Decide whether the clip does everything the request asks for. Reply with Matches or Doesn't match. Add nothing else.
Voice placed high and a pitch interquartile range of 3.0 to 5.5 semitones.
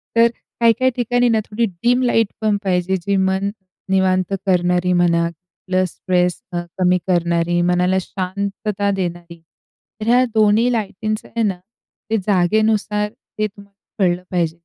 Matches